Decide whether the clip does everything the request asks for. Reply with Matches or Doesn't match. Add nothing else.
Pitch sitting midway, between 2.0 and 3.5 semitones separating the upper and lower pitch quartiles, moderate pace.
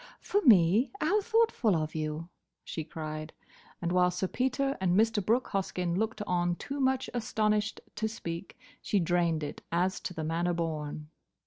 Doesn't match